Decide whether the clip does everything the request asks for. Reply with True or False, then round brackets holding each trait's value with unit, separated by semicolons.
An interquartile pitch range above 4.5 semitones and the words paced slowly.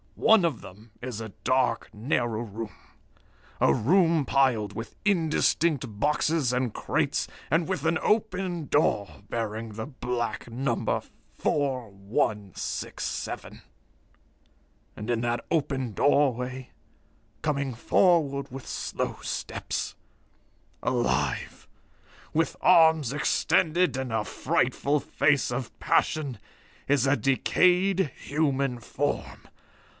True (5.1 semitones; 100 wpm)